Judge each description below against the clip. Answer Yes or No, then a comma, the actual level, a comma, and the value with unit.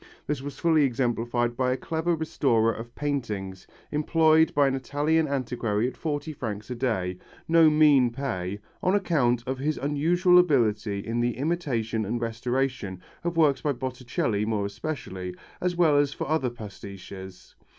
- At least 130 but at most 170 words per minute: Yes, average, 155 wpm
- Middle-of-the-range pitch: No, low, 130 Hz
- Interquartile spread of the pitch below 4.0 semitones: No, average, 5.2 semitones